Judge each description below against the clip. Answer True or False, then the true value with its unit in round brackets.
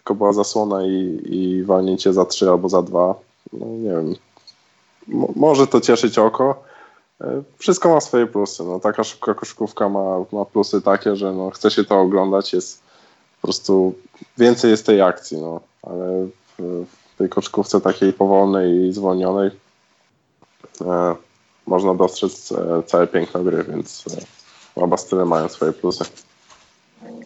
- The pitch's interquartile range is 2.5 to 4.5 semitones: True (2.9 semitones)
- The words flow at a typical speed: True (150 wpm)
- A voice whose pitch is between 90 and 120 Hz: True (95 Hz)